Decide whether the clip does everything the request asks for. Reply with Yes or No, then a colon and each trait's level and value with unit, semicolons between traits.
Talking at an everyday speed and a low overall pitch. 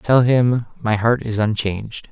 Yes: average, 170 wpm; low, 115 Hz